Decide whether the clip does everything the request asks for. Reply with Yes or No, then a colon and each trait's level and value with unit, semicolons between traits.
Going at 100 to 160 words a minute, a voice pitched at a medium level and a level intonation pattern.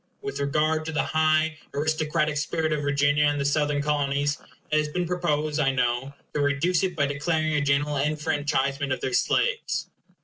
No: average, 175 wpm; medium, 150 Hz; narrow, 1.6 semitones